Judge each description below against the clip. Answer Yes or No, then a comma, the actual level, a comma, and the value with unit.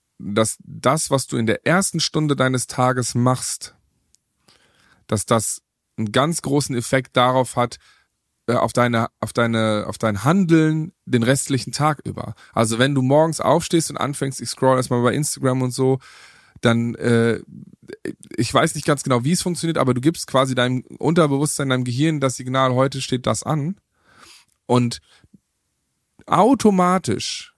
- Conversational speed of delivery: Yes, average, 155 wpm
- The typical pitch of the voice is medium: No, low, 130 Hz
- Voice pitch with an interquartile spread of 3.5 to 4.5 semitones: Yes, average, 4.0 semitones